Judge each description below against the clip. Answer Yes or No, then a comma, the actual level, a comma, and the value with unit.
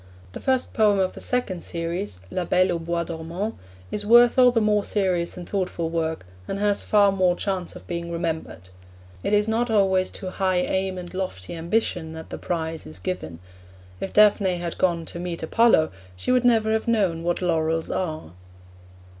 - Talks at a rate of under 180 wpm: No, average, 185 wpm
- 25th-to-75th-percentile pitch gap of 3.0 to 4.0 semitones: Yes, average, 3.7 semitones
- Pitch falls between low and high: Yes, medium, 180 Hz